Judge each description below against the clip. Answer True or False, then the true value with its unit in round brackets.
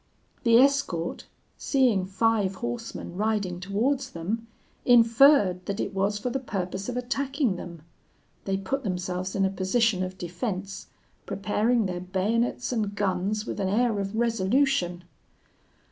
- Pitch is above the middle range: True (205 Hz)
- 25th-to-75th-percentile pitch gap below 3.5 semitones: False (4.2 semitones)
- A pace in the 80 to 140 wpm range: True (135 wpm)